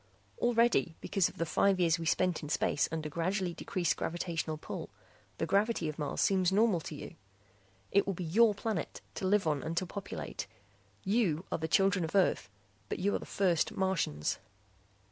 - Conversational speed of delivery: Yes, average, 185 wpm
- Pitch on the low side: No, medium, 180 Hz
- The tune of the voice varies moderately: Yes, average, 3.6 semitones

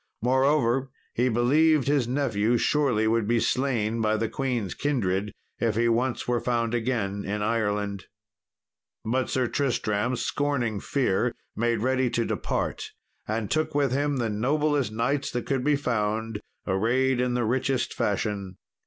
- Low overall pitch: Yes, low, 120 Hz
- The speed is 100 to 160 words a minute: Yes, average, 145 wpm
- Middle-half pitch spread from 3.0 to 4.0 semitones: Yes, average, 3.4 semitones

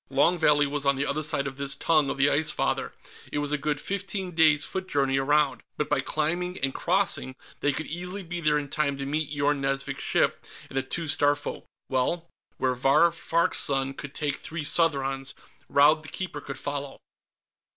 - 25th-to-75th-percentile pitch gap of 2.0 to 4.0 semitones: Yes, narrow, 2.6 semitones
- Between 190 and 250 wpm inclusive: Yes, average, 195 wpm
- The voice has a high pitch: No, medium, 145 Hz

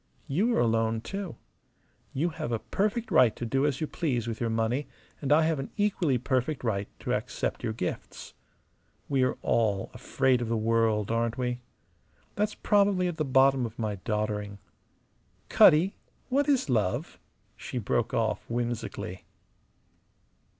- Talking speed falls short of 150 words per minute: No, average, 155 wpm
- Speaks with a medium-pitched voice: No, low, 125 Hz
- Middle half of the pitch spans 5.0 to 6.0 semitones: Yes, wide, 5.6 semitones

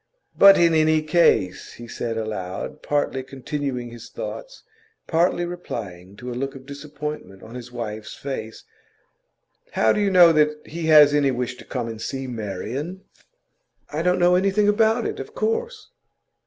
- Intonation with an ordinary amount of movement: No, wide, 6.6 semitones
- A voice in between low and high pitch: Yes, medium, 145 Hz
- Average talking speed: Yes, average, 160 wpm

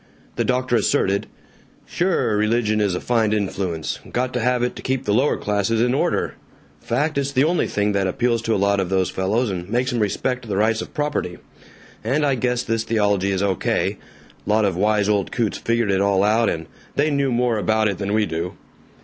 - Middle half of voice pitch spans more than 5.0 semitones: No, average, 3.7 semitones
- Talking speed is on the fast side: Yes, fast, 210 wpm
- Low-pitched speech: Yes, low, 110 Hz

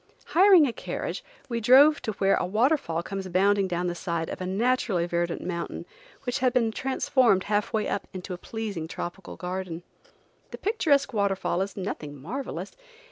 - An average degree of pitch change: No, wide, 5.7 semitones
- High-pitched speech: Yes, high, 200 Hz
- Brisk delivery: No, average, 170 wpm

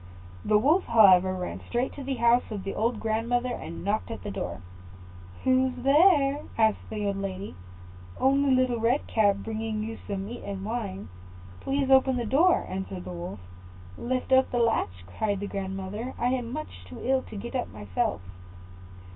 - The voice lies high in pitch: Yes, high, 225 Hz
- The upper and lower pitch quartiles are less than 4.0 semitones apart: No, average, 4.7 semitones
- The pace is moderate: Yes, average, 175 wpm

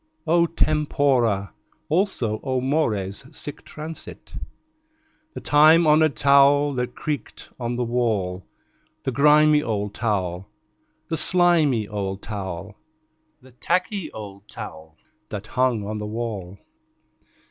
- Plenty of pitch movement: Yes, wide, 6.6 semitones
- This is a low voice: Yes, low, 125 Hz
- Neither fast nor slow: No, slow, 115 wpm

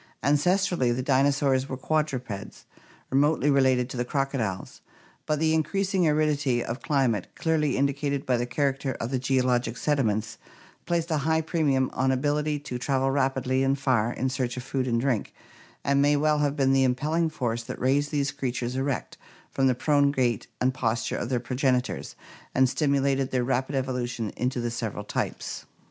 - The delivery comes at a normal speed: Yes, average, 170 wpm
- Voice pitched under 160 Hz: Yes, low, 135 Hz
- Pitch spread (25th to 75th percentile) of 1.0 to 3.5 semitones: Yes, narrow, 2.5 semitones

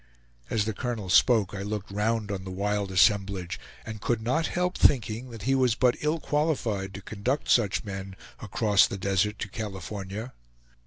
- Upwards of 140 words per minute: Yes, average, 170 wpm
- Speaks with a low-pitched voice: Yes, low, 105 Hz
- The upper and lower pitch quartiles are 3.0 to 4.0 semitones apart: Yes, average, 3.5 semitones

